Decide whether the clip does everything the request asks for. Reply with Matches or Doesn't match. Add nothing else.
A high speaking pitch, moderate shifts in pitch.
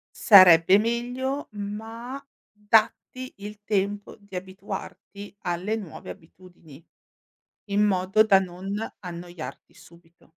Matches